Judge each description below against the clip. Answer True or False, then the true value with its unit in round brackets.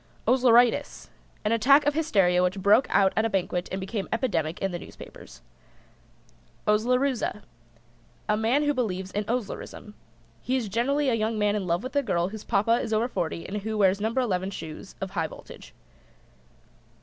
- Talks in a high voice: True (215 Hz)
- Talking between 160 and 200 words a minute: True (175 wpm)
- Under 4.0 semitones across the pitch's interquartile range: False (4.3 semitones)